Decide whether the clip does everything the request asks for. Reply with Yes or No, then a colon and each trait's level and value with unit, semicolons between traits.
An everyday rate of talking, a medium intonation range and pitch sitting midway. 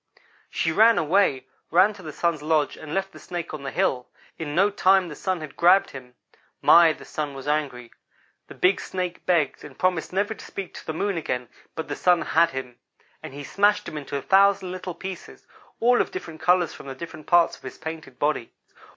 No: fast, 210 wpm; average, 4.0 semitones; medium, 165 Hz